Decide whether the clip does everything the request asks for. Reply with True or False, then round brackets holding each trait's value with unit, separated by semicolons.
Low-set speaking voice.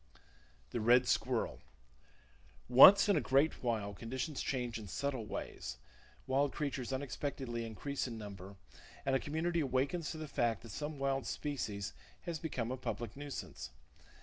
True (130 Hz)